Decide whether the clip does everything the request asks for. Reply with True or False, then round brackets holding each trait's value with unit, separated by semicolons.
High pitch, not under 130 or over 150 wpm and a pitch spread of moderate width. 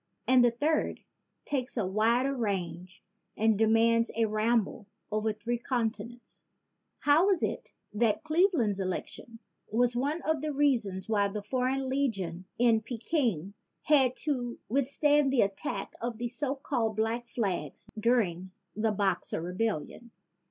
True (230 Hz; 140 wpm; 3.9 semitones)